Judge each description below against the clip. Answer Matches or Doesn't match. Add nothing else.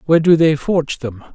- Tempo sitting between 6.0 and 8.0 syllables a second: Matches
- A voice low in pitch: Doesn't match